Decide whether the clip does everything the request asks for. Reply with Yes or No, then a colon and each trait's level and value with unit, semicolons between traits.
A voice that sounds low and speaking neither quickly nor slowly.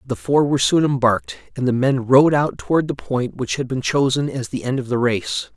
No: low, 130 Hz; fast, 250 wpm